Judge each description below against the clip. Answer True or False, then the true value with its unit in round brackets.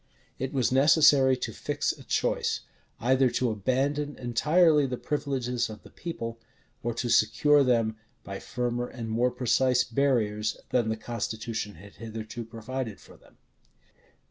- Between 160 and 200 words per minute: False (145 wpm)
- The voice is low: True (120 Hz)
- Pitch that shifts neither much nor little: True (3.0 semitones)